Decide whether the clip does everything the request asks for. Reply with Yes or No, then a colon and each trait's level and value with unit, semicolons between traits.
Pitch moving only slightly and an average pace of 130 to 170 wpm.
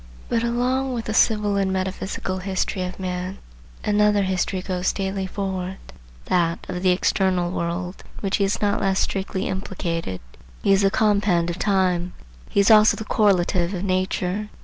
Yes: narrow, 2.1 semitones; average, 160 wpm